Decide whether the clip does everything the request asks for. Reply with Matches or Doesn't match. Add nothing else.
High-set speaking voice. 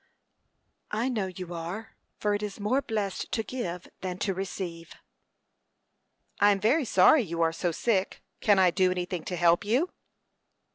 Matches